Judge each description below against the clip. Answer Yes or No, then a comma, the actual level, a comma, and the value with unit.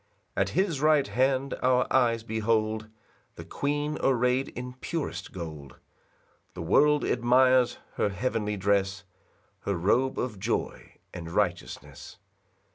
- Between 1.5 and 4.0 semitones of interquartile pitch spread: No, average, 4.6 semitones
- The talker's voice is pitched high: No, low, 120 Hz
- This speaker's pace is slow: Yes, slow, 120 wpm